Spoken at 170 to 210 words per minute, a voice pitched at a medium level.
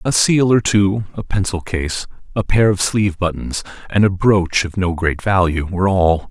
No: average, 200 wpm; very low, 95 Hz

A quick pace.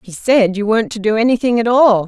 Yes: fast, 260 wpm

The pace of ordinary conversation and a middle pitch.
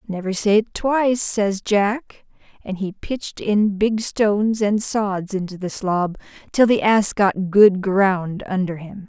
No: average, 160 wpm; high, 200 Hz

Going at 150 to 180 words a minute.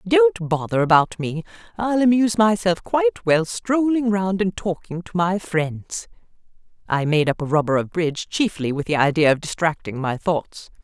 Yes: average, 170 wpm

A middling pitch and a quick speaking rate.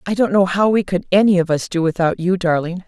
Yes: medium, 180 Hz; fast, 270 wpm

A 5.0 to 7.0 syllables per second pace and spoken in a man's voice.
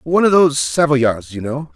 Yes: 5.3 syllables/s; male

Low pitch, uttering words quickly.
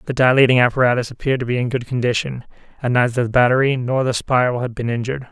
Yes: low, 125 Hz; fast, 215 wpm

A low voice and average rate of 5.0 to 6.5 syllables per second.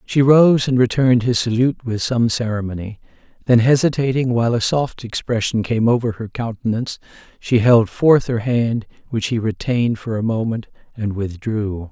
Yes: low, 115 Hz; 5.1 syllables/s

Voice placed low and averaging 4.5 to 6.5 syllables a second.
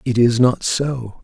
No: low, 120 Hz; 3.7 syllables/s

